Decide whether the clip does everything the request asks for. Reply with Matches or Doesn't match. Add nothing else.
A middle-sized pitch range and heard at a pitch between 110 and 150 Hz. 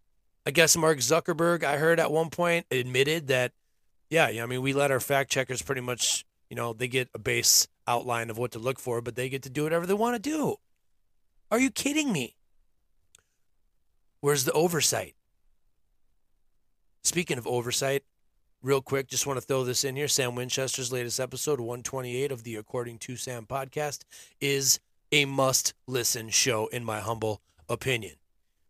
Matches